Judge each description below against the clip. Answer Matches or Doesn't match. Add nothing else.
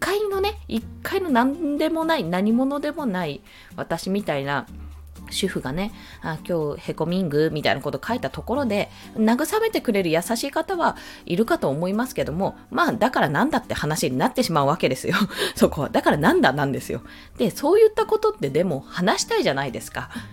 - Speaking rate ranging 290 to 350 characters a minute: Doesn't match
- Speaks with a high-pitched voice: Matches